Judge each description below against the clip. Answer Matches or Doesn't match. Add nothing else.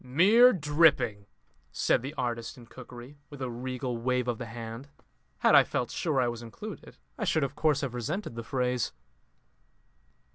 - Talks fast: Doesn't match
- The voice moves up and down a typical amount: Matches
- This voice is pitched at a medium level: Doesn't match